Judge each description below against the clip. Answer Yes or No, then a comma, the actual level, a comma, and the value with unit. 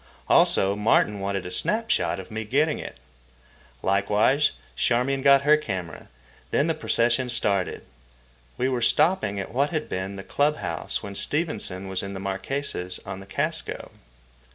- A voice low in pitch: Yes, low, 110 Hz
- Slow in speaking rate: No, average, 155 wpm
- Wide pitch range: Yes, wide, 6.4 semitones